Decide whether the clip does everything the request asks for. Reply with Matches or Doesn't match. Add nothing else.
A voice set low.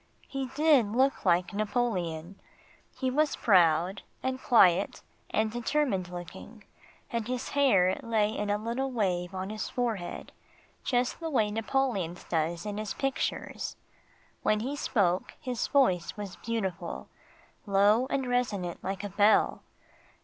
Doesn't match